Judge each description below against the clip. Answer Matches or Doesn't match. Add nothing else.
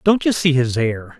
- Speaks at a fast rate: Matches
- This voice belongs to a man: Matches